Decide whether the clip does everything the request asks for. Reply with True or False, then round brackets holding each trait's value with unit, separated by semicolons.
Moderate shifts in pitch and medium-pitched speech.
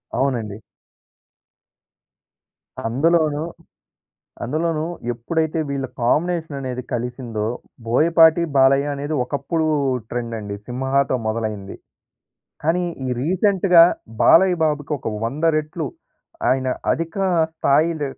True (4.7 semitones; 145 Hz)